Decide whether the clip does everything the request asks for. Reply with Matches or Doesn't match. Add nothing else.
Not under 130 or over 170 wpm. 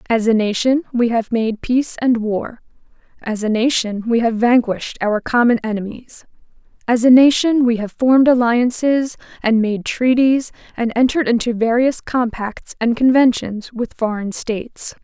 Matches